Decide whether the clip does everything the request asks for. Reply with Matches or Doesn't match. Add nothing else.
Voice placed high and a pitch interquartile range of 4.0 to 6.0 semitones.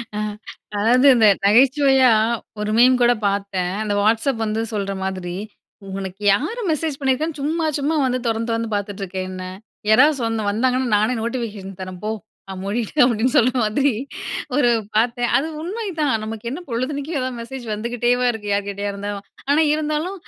Matches